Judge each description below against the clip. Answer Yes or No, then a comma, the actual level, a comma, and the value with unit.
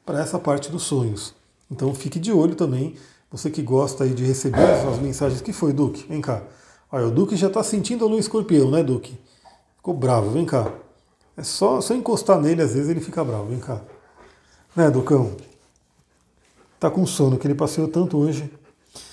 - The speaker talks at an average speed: No, fast, 190 wpm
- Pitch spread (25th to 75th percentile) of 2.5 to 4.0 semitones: No, average, 4.4 semitones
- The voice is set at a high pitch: No, medium, 145 Hz